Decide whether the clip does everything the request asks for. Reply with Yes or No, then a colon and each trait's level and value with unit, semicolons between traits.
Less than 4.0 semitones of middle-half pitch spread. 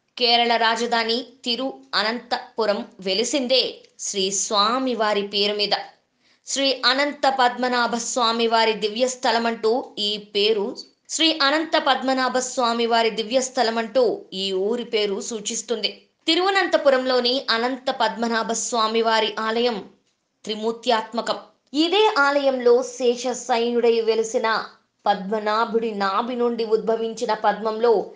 Yes: narrow, 2.6 semitones